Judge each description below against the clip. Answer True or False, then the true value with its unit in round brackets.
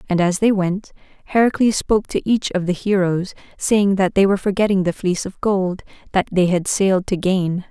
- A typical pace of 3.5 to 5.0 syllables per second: False (5.4 syllables/s)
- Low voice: False (190 Hz)